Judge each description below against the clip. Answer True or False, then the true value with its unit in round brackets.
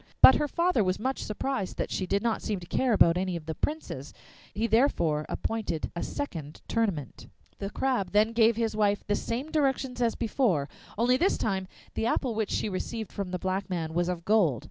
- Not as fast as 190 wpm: False (205 wpm)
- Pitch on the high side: True (210 Hz)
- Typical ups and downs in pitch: True (4.6 semitones)